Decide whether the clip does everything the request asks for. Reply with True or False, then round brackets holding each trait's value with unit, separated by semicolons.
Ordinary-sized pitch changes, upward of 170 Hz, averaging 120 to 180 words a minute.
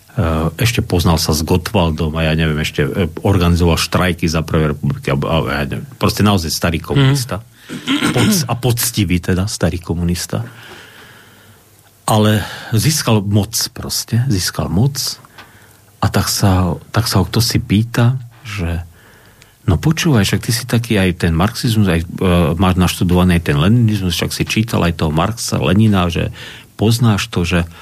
False (4.5 semitones; 105 Hz; 140 wpm)